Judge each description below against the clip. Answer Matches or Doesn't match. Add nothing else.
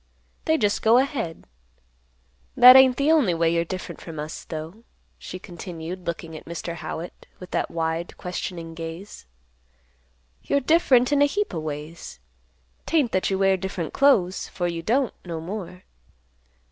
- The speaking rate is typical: Matches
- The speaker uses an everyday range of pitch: Doesn't match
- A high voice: Doesn't match